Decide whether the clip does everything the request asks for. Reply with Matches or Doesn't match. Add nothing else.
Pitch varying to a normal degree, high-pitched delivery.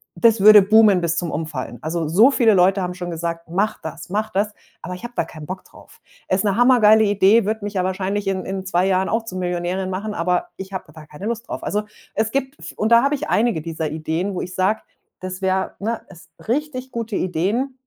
Matches